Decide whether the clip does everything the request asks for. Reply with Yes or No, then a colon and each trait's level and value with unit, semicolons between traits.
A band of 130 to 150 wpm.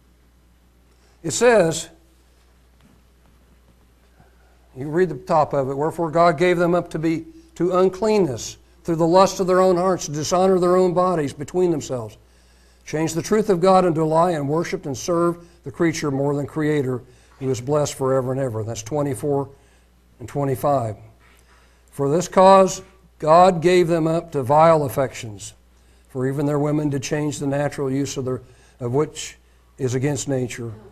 No: average, 165 wpm